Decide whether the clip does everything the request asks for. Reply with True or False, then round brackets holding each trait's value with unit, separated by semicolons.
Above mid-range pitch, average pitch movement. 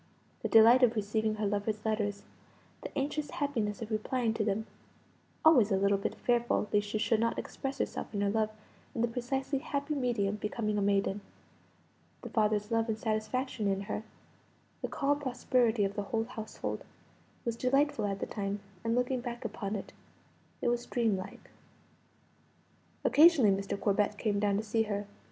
True (220 Hz; 3.1 semitones)